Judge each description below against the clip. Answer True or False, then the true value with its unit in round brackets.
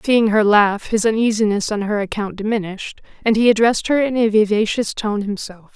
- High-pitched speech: True (215 Hz)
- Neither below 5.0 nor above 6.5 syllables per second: True (5.6 syllables/s)